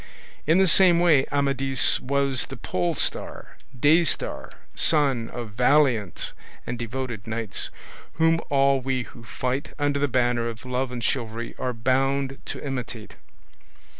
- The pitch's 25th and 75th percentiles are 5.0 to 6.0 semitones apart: No, average, 3.1 semitones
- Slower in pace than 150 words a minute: Yes, slow, 135 wpm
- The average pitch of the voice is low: Yes, low, 130 Hz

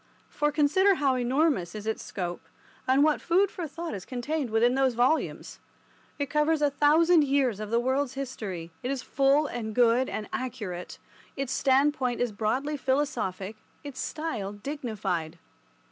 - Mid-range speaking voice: No, very high, 260 Hz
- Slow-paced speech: No, average, 155 wpm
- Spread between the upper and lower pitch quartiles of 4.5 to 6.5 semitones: Yes, average, 5.0 semitones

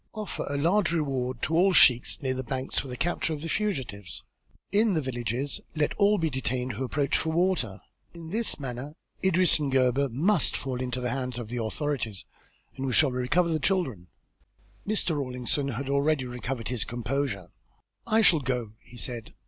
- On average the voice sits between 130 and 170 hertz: Yes, low, 135 Hz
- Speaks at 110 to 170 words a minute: No, average, 180 wpm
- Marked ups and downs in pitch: No, average, 4.6 semitones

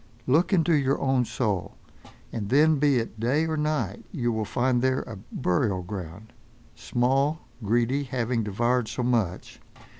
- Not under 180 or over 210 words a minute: No, average, 150 wpm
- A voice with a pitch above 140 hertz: No, low, 125 Hz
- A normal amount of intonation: Yes, average, 4.0 semitones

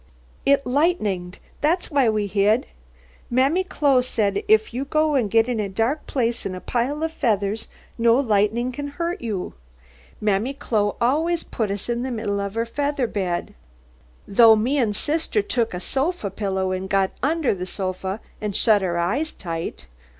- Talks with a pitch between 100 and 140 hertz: No, high, 230 Hz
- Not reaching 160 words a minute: No, average, 170 wpm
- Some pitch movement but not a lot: No, wide, 5.8 semitones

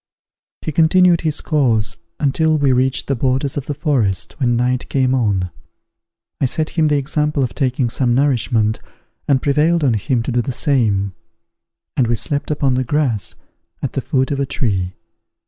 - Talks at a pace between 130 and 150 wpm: No, average, 175 wpm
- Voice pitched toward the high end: No, low, 130 Hz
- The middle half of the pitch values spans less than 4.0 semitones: Yes, average, 3.6 semitones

